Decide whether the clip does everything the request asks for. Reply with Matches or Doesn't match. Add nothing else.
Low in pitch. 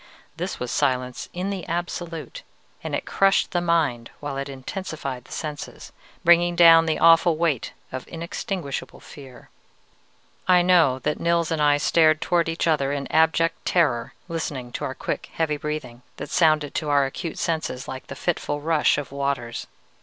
Doesn't match